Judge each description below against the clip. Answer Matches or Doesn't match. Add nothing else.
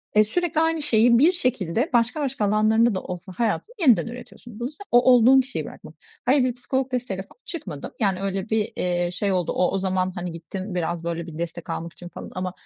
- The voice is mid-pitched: Doesn't match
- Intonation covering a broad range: Matches